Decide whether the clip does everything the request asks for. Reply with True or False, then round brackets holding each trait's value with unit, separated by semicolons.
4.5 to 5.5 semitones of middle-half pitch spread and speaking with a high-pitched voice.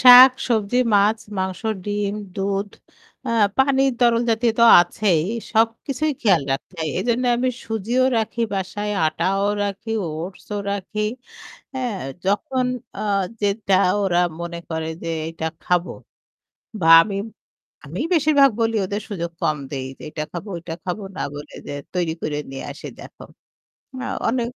True (5.0 semitones; 205 Hz)